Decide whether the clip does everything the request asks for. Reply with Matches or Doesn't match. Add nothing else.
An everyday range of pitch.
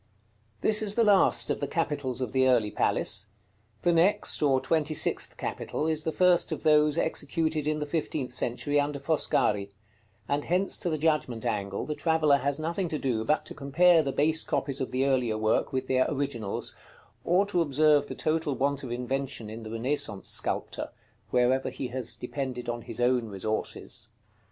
Matches